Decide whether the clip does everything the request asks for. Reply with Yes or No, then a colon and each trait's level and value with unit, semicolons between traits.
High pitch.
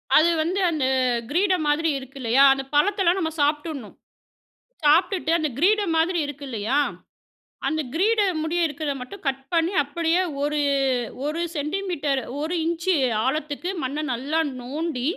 Yes: very high, 315 Hz